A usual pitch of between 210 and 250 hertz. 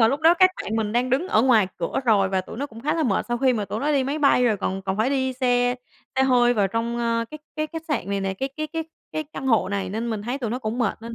Yes: high, 240 Hz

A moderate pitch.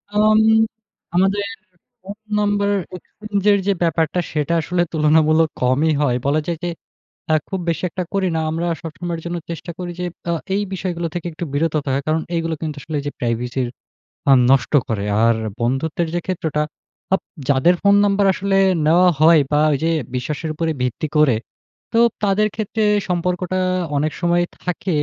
Yes: medium, 165 Hz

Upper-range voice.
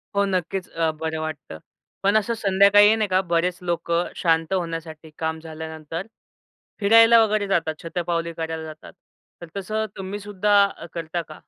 No: medium, 175 Hz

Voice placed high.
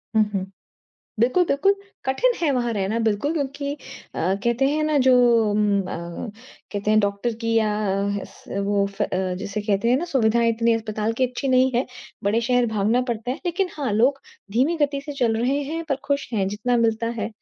Yes: high, 235 Hz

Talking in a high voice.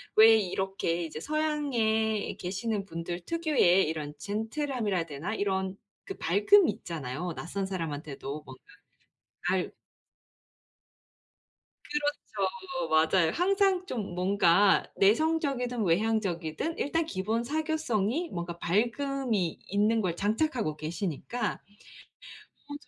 Yes: high, 205 Hz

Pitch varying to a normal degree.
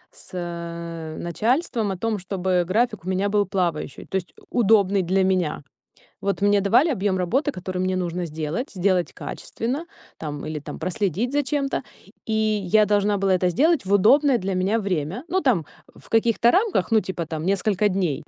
Yes: average, 3.8 semitones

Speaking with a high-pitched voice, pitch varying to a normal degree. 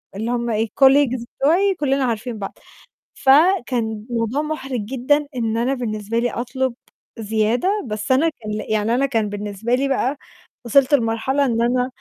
Yes: high, 245 Hz; average, 3.4 semitones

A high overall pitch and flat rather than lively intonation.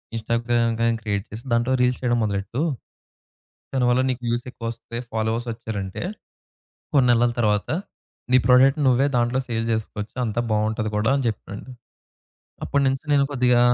No: low, 120 Hz; narrow, 2.3 semitones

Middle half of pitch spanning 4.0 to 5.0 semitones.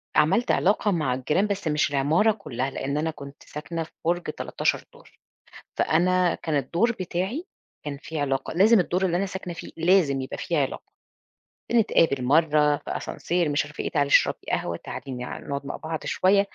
Yes: average, 4.6 semitones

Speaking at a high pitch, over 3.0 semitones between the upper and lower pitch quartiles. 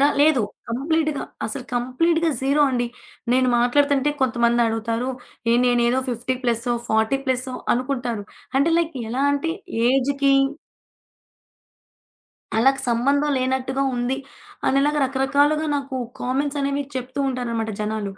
No: very high, 260 Hz; average, 2.7 semitones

